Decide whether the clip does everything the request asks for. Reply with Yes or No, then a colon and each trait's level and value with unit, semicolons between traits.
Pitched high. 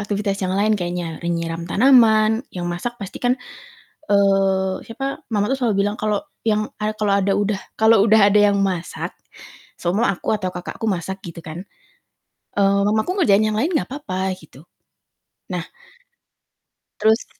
Yes: high, 205 Hz